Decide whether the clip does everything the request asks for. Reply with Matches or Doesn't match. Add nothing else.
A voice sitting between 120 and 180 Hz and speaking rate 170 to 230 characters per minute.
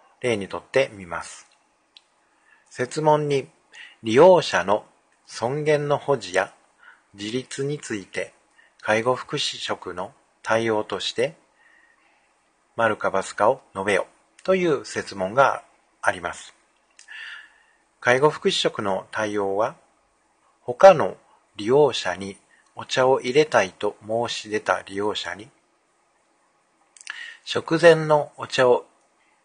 Matches